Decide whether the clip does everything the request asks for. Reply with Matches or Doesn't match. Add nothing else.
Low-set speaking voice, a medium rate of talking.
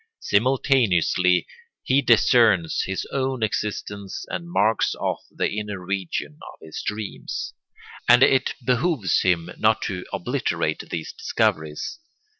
Doesn't match